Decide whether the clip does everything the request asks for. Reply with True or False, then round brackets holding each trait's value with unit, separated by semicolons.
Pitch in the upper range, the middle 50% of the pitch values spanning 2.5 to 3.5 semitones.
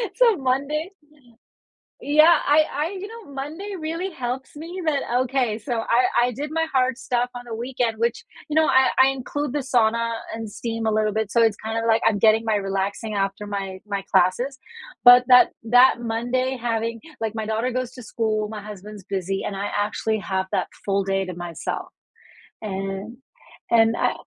False (230 Hz; 3.9 semitones)